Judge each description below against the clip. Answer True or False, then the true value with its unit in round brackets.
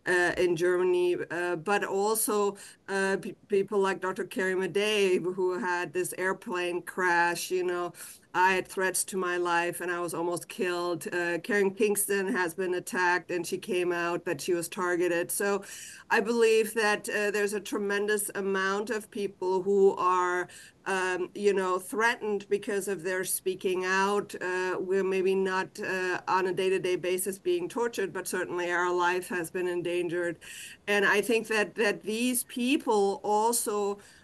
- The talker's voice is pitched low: False (185 Hz)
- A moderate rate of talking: True (165 wpm)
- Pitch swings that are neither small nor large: False (2.2 semitones)